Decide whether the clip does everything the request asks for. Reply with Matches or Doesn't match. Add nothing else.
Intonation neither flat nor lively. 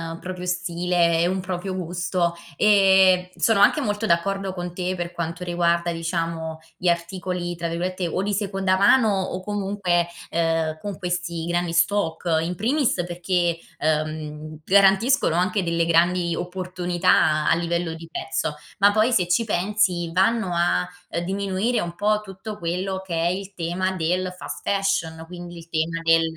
Doesn't match